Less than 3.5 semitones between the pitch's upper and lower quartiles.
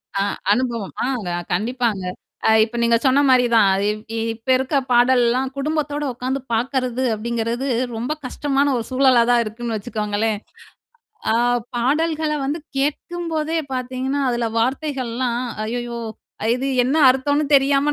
Yes: average, 2.8 semitones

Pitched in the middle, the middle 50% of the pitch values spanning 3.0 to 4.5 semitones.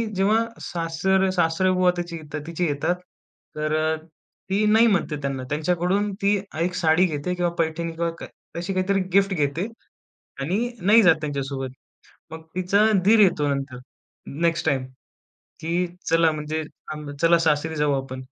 Yes: medium, 165 Hz; average, 3.6 semitones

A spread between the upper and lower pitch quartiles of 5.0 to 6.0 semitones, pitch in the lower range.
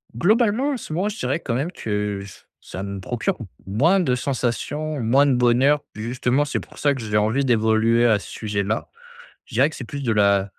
Yes: average, 5.3 semitones; low, 125 Hz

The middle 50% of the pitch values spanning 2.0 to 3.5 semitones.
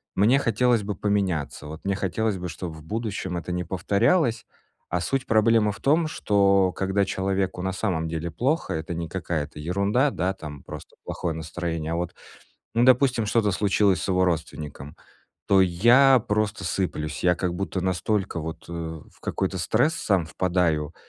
No: average, 4.1 semitones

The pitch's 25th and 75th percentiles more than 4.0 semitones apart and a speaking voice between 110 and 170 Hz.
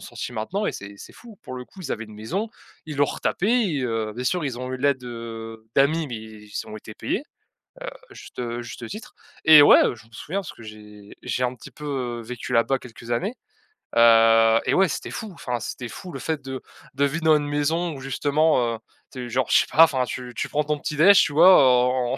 Yes: average, 4.7 semitones; low, 130 Hz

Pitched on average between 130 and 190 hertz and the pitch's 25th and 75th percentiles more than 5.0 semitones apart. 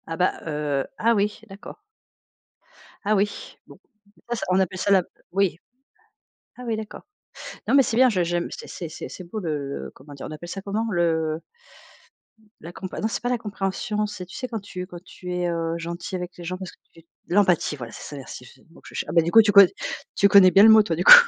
No: medium, 185 Hz; average, 3.7 semitones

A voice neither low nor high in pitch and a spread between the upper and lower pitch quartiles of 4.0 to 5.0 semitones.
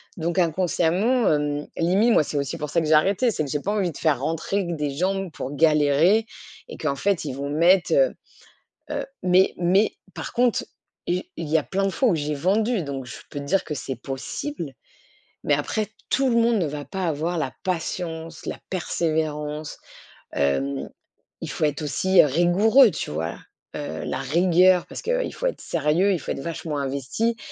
Yes: medium, 165 Hz; average, 4.7 semitones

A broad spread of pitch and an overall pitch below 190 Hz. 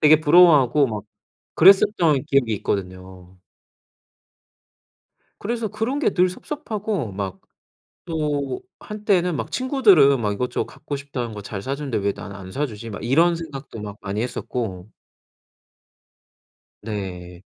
Yes: wide, 8.8 semitones; low, 135 Hz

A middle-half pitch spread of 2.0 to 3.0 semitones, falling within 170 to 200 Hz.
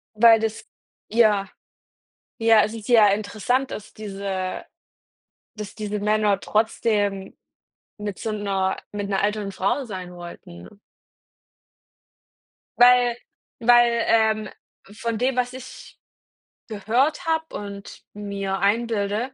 No: narrow, 2.6 semitones; high, 215 Hz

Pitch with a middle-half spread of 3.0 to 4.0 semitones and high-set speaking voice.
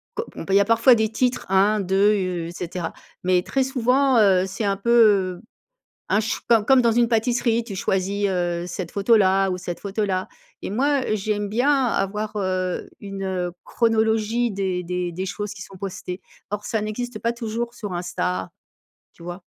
Yes: average, 3.6 semitones; high, 205 Hz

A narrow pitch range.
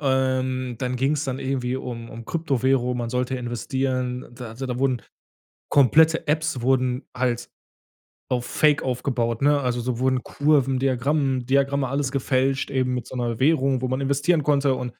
Yes: narrow, 1.7 semitones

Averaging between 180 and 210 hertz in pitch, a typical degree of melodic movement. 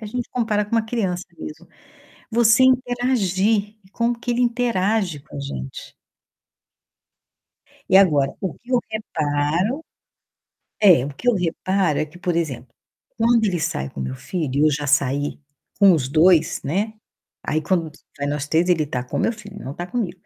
No: medium, 185 Hz; wide, 6.9 semitones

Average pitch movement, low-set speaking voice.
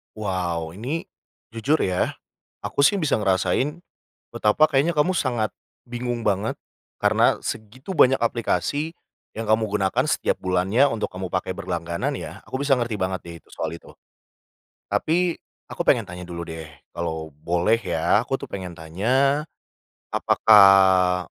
No: wide, 6.3 semitones; low, 105 Hz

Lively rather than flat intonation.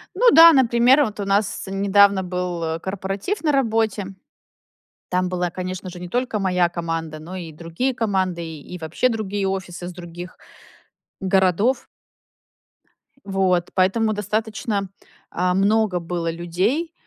No: average, 3.5 semitones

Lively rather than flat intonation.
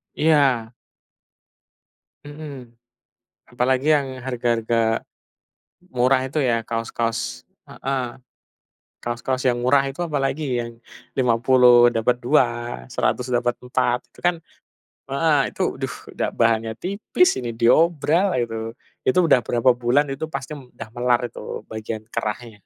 No: average, 2.7 semitones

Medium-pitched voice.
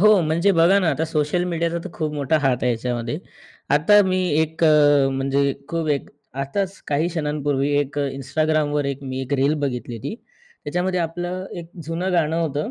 Yes: medium, 150 Hz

